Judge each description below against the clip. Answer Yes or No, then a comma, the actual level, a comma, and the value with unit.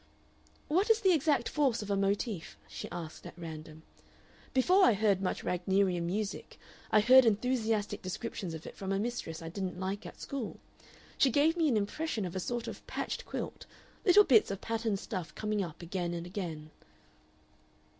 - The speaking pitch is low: No, high, 200 Hz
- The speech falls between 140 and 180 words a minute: Yes, average, 175 wpm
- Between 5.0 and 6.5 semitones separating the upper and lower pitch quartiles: Yes, wide, 5.5 semitones